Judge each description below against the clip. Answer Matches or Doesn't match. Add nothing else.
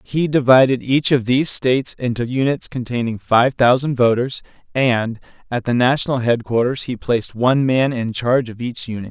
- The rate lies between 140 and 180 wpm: Matches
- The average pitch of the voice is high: Doesn't match